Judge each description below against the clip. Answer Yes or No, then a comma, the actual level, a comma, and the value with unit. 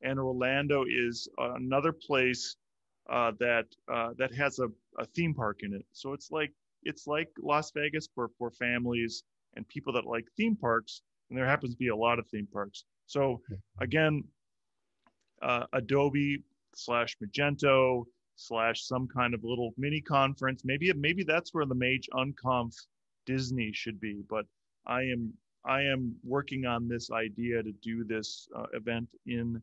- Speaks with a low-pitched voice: Yes, low, 125 Hz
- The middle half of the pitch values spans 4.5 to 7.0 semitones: No, average, 3.1 semitones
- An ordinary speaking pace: Yes, average, 160 wpm